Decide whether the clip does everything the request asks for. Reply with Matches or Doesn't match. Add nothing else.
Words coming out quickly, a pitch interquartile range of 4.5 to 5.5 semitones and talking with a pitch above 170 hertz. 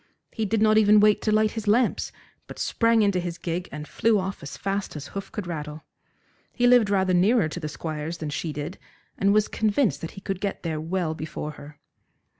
Matches